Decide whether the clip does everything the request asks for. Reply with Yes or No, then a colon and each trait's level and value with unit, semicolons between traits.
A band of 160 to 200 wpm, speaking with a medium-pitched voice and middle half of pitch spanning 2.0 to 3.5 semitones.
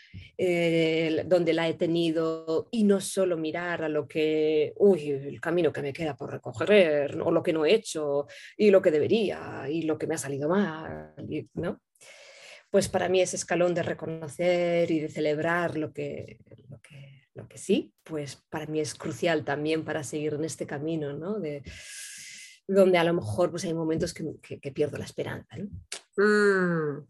Yes: average, 185 wpm; medium, 160 Hz; average, 3.0 semitones